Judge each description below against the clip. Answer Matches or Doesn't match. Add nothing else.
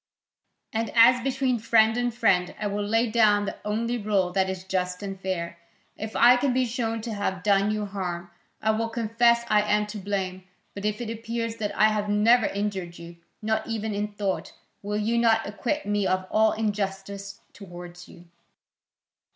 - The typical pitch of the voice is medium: Doesn't match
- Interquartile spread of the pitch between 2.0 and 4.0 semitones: Matches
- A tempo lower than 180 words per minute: Doesn't match